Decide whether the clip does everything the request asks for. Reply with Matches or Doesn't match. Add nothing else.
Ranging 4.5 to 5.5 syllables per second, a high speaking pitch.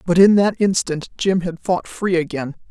Doesn't match